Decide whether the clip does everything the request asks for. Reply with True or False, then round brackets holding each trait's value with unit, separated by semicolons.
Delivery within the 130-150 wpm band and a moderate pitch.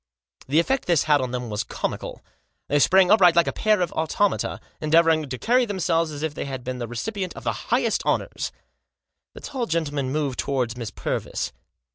False (190 wpm; 155 Hz)